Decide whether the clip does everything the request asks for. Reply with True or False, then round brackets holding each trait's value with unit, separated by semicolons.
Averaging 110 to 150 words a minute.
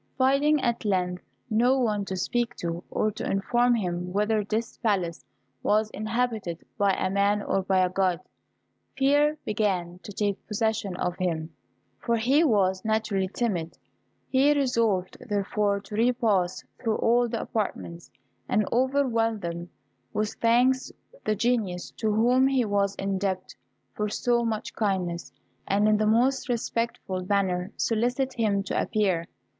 True (140 wpm)